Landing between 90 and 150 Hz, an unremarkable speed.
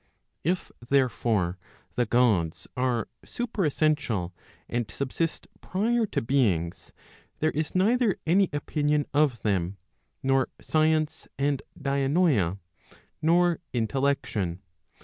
No: medium, 140 Hz; slow, 95 wpm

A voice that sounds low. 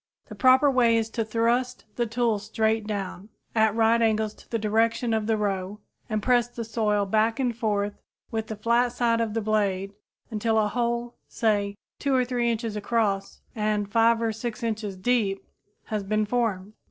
No: high, 220 Hz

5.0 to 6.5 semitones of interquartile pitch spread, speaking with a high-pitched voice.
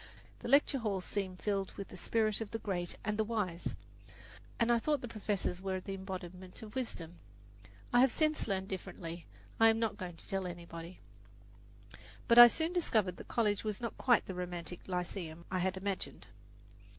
No: average, 3.8 semitones; high, 195 Hz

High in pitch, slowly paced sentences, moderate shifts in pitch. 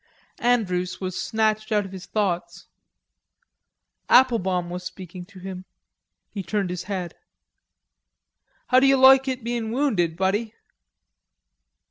Yes: high, 200 Hz; slow, 115 wpm; average, 4.4 semitones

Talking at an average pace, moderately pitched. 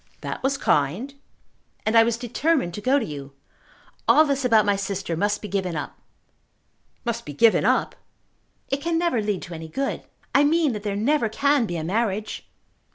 No: average, 185 wpm; high, 220 Hz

